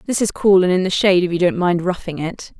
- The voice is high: No, medium, 180 Hz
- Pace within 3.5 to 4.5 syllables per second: No, 6.3 syllables/s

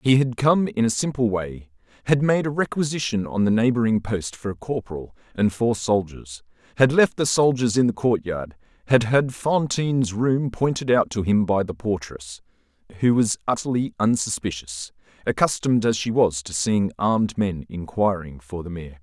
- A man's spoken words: Yes, male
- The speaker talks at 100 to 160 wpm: No, average, 175 wpm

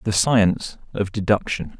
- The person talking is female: No, male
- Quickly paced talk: No, slow, 135 wpm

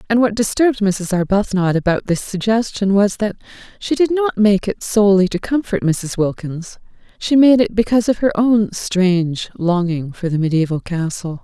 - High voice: Yes, high, 200 Hz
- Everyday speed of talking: Yes, average, 175 wpm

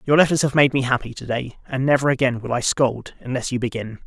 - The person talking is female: No, male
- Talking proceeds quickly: Yes, fast, 250 wpm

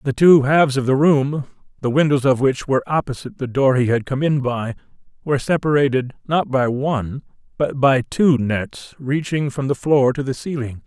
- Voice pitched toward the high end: No, low, 135 Hz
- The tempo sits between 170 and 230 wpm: Yes, average, 195 wpm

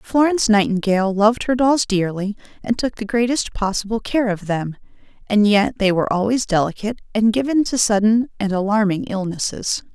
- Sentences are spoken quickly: No, average, 165 wpm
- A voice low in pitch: No, high, 215 Hz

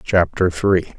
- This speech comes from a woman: No, male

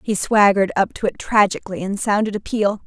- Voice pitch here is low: No, high, 200 Hz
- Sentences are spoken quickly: Yes, fast, 210 wpm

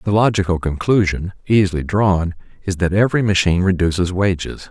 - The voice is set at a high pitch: No, very low, 95 Hz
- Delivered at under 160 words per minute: Yes, average, 140 wpm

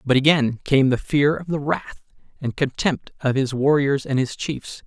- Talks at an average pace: Yes, average, 195 wpm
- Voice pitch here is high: No, low, 135 Hz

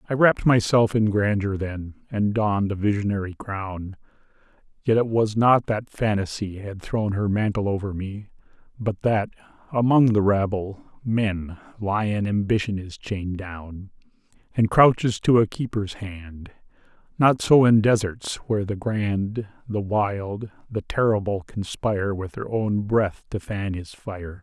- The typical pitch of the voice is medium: No, low, 105 Hz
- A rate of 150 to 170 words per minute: No, average, 140 wpm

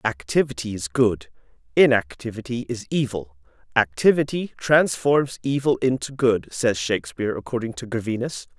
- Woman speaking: No, male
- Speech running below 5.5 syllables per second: Yes, 5.0 syllables/s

